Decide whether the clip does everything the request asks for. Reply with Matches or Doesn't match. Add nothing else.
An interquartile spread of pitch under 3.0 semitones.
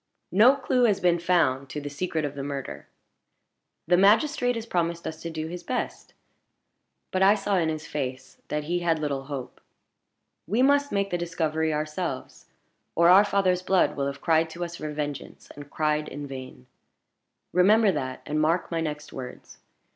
Doesn't match